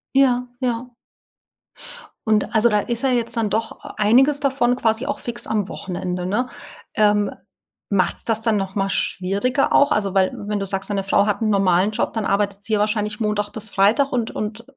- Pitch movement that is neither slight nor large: Yes, average, 3.0 semitones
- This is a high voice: Yes, high, 215 Hz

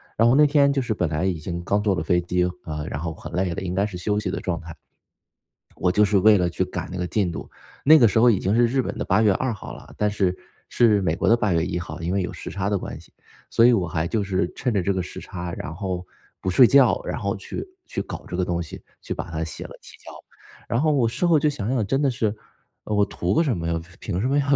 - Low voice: Yes, low, 100 Hz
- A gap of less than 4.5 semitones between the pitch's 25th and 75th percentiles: No, average, 4.8 semitones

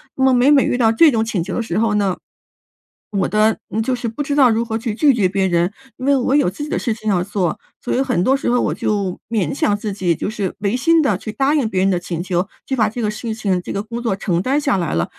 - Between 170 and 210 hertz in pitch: No, high, 220 Hz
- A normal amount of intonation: Yes, average, 4.5 semitones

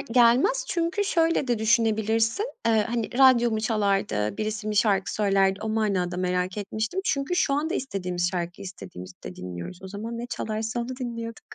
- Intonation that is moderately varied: Yes, average, 3.8 semitones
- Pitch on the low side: No, high, 220 Hz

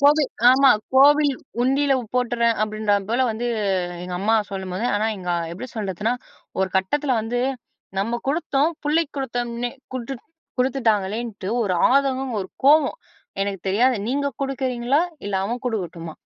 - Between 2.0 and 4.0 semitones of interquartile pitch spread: No, average, 4.7 semitones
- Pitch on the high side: Yes, high, 240 Hz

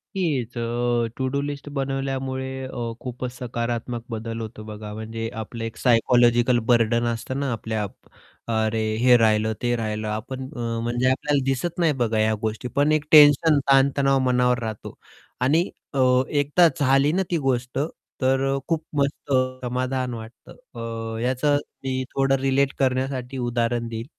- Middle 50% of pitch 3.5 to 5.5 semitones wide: No, average, 2.9 semitones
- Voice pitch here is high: No, low, 125 Hz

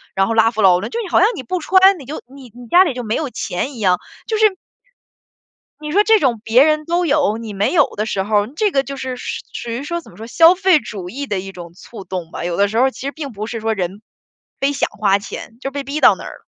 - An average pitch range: No, wide, 6.6 semitones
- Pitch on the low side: No, very high, 250 Hz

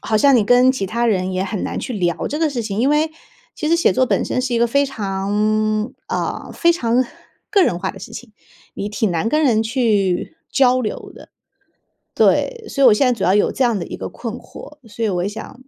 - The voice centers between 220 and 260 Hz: Yes, high, 230 Hz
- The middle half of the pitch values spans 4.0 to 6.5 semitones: Yes, average, 4.3 semitones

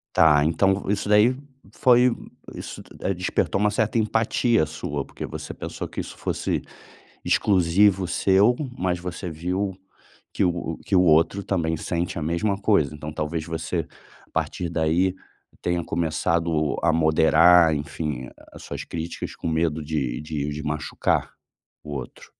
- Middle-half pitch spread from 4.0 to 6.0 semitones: No, average, 3.6 semitones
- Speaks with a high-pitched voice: No, very low, 85 Hz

